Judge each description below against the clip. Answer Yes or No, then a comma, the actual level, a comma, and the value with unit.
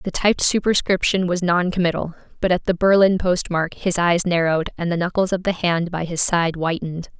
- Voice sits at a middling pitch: Yes, medium, 175 Hz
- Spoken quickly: No, average, 190 wpm